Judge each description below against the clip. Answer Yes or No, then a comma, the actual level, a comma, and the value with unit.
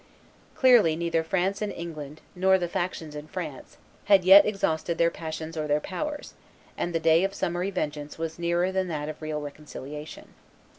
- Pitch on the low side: No, medium, 170 Hz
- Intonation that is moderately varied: Yes, average, 3.4 semitones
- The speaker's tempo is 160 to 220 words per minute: Yes, average, 170 wpm